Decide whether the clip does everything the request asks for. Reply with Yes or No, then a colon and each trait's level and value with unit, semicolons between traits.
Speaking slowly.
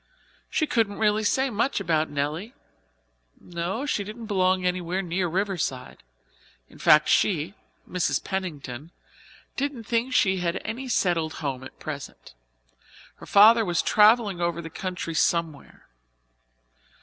Yes: slow, 130 wpm